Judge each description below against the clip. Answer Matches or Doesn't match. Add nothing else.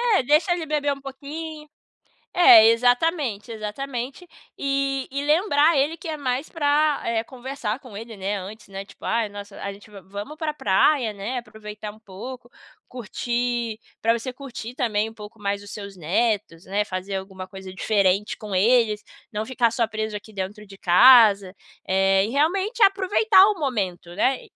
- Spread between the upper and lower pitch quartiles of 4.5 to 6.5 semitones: Matches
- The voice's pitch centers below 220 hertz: Doesn't match